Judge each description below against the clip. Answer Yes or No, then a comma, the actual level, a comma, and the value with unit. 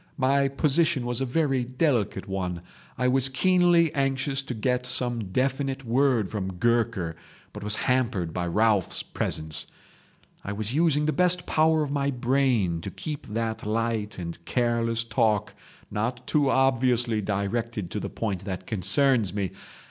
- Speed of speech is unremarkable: Yes, average, 150 wpm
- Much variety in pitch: No, average, 4.6 semitones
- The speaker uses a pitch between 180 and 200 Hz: No, low, 120 Hz